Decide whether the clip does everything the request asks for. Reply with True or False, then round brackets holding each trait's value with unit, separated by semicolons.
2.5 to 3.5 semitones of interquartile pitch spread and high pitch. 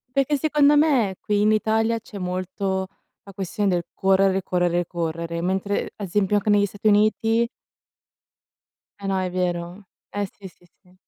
True (2.8 semitones; 195 Hz)